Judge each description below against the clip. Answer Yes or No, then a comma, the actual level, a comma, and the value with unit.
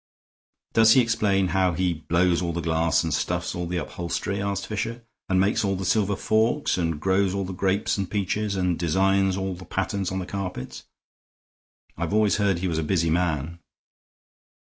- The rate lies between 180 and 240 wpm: Yes, average, 185 wpm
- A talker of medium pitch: No, very low, 95 Hz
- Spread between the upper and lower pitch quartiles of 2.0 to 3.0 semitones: Yes, narrow, 2.5 semitones